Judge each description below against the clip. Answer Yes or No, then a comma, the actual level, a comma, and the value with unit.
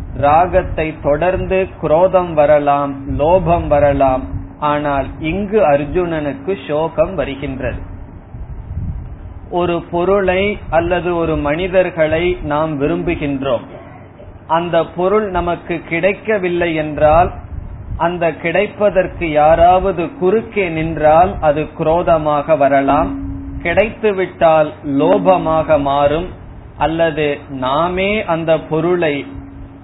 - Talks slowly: Yes, slow, 70 wpm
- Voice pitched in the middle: Yes, medium, 155 Hz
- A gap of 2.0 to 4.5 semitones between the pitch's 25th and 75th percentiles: Yes, average, 3.8 semitones